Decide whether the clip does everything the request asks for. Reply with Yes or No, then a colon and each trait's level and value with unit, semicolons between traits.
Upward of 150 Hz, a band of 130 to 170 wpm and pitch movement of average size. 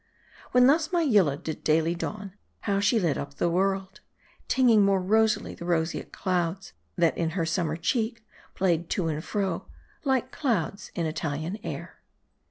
Yes: high, 190 Hz; average, 160 wpm; average, 4.8 semitones